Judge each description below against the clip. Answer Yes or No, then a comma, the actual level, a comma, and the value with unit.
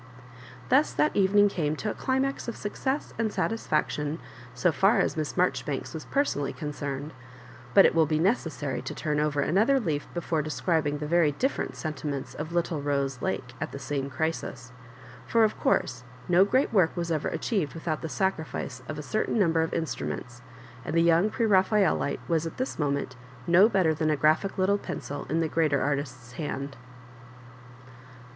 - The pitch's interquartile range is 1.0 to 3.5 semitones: No, average, 4.9 semitones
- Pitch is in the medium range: Yes, medium, 160 Hz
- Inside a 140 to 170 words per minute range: No, average, 180 wpm